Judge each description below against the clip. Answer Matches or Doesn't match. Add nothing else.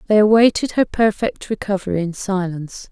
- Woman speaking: Matches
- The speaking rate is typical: Matches